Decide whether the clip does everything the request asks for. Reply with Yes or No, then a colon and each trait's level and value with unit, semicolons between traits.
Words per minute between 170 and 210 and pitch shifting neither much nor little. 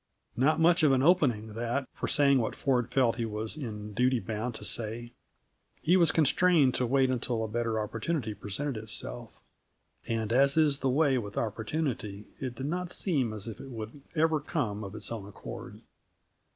Yes: average, 180 wpm; average, 4.6 semitones